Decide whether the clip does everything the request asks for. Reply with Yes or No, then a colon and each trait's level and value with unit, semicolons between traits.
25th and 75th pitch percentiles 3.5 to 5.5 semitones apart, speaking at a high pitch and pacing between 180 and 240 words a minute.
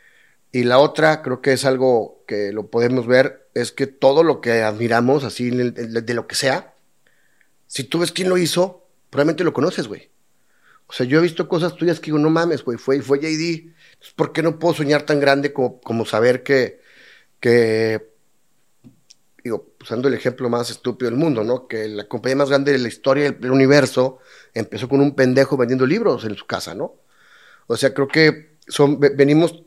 No: average, 4.0 semitones; low, 135 Hz; fast, 190 wpm